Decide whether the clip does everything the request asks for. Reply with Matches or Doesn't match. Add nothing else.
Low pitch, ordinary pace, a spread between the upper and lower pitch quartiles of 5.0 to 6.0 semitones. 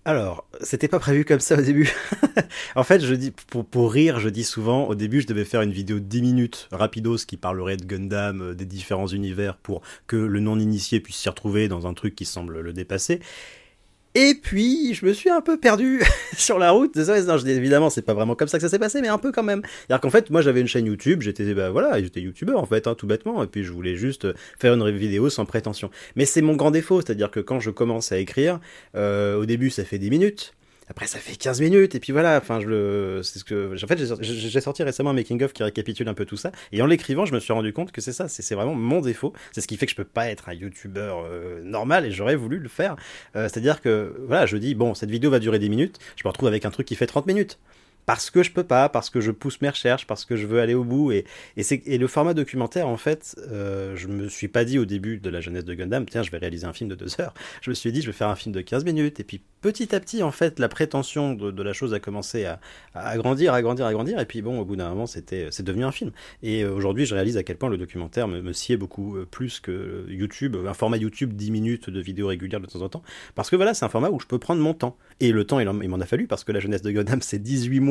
Doesn't match